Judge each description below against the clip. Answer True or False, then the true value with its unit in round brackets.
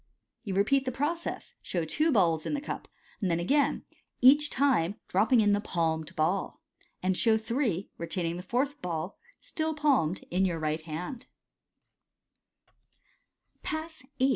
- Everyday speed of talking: True (150 wpm)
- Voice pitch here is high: True (205 Hz)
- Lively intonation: True (8.4 semitones)